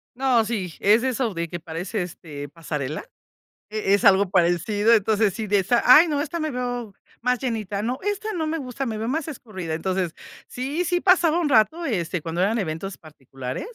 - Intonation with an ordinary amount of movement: No, wide, 6.6 semitones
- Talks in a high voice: Yes, high, 215 Hz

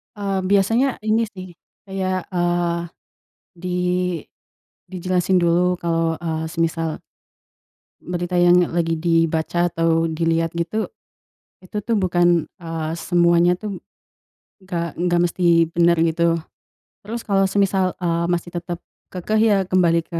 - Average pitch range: No, narrow, 1.9 semitones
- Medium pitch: Yes, medium, 175 Hz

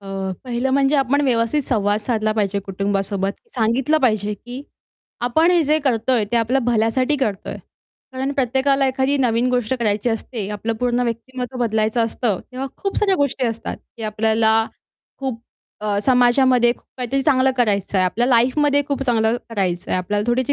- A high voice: Yes, high, 240 Hz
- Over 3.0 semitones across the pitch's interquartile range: Yes, average, 3.6 semitones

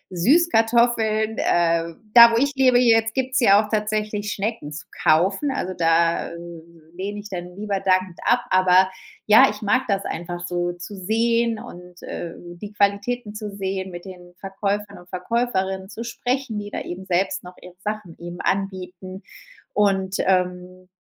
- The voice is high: Yes, high, 195 Hz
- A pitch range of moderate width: Yes, average, 3.5 semitones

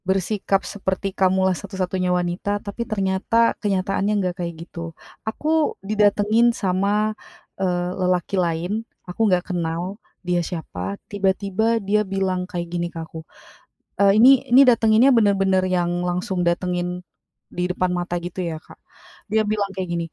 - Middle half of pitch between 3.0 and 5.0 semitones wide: No, narrow, 2.4 semitones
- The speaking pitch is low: No, high, 190 Hz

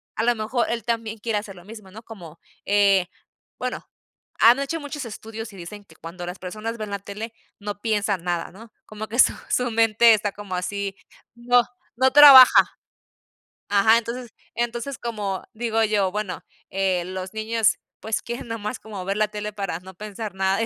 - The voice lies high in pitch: Yes, high, 215 Hz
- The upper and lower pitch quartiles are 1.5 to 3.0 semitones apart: Yes, average, 2.7 semitones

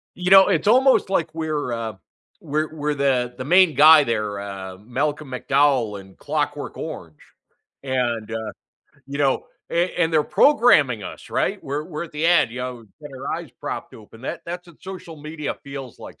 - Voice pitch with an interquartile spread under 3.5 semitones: No, average, 4.8 semitones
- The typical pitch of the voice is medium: Yes, medium, 145 Hz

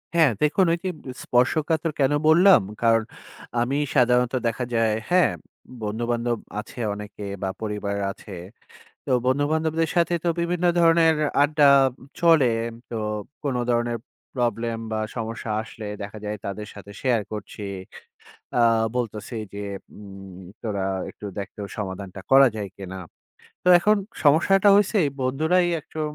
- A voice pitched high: No, low, 120 Hz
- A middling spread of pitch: No, wide, 6.9 semitones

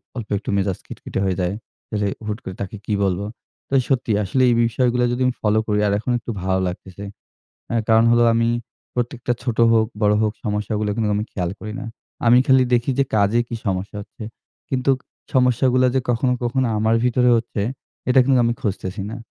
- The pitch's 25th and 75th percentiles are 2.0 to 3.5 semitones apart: Yes, average, 3.1 semitones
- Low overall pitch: Yes, low, 115 Hz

